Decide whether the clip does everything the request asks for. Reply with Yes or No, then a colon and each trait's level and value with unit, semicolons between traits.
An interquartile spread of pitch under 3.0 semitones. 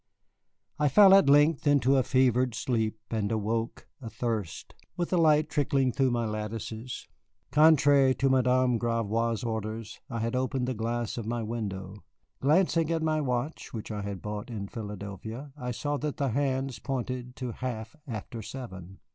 No: average, 3.7 semitones